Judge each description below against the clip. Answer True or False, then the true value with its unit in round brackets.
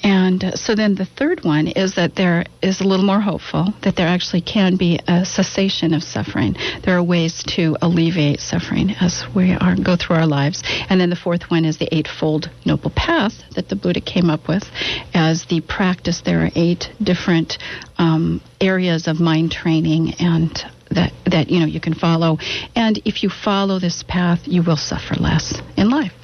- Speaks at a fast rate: False (190 wpm)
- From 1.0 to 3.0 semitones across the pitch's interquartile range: True (2.6 semitones)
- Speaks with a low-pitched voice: False (175 Hz)